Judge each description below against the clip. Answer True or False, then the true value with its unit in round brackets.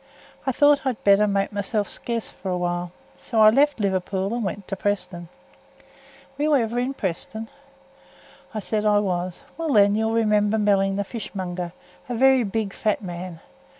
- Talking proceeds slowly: False (175 wpm)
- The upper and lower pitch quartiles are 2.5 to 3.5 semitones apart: True (3.1 semitones)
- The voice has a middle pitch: False (205 Hz)